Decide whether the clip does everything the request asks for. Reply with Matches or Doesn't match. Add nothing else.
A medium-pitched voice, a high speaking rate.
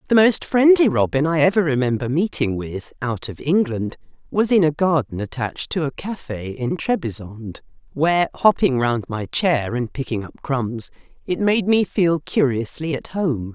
Doesn't match